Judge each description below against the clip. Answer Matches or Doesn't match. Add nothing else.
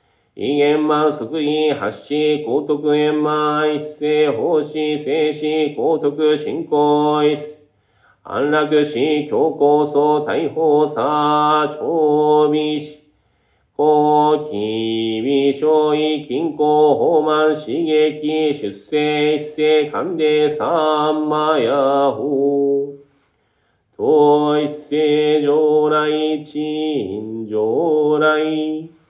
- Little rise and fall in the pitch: Matches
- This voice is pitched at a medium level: Matches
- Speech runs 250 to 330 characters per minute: Doesn't match